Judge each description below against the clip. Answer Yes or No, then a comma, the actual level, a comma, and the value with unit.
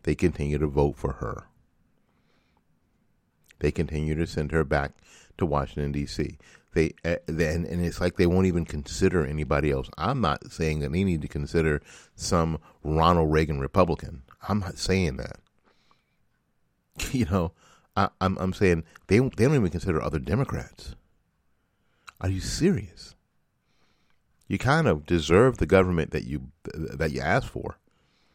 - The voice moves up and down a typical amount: Yes, average, 3.7 semitones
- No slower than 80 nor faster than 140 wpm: No, average, 150 wpm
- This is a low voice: Yes, very low, 80 Hz